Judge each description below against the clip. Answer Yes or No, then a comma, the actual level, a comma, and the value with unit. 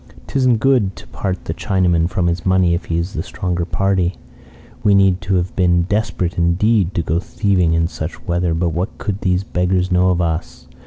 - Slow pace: No, average, 195 wpm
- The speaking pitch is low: Yes, very low, 90 Hz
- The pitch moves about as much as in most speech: No, narrow, 2.1 semitones